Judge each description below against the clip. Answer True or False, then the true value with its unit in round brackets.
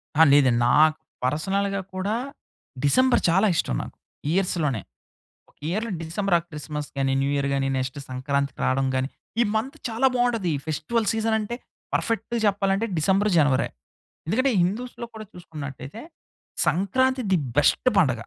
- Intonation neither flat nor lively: False (7.7 semitones)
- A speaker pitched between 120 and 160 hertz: False (180 Hz)